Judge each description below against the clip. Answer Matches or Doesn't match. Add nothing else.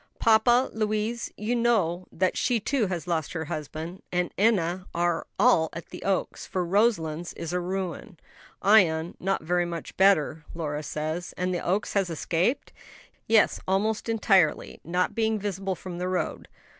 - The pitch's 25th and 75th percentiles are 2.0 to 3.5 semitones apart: Doesn't match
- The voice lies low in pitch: Doesn't match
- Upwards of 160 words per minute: Doesn't match